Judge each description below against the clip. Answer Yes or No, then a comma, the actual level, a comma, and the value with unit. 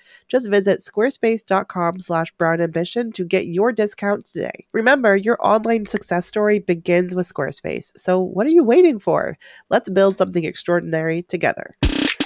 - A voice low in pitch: No, high, 195 Hz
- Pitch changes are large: No, average, 4.0 semitones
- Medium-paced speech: Yes, average, 145 wpm